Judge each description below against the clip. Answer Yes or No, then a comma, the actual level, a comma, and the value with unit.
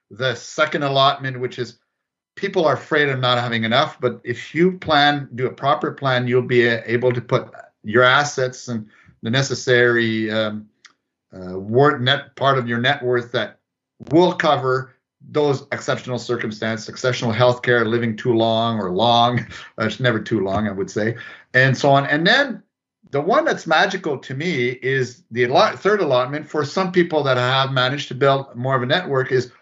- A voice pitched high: No, low, 125 Hz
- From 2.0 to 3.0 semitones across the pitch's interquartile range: Yes, narrow, 2.6 semitones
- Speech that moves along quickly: No, average, 180 wpm